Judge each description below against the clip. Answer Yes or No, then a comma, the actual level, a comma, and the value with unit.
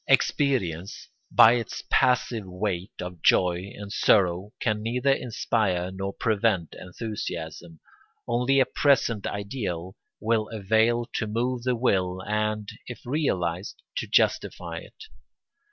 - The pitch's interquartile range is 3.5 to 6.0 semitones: Yes, average, 4.4 semitones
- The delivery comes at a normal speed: No, slow, 120 wpm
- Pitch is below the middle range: Yes, low, 105 Hz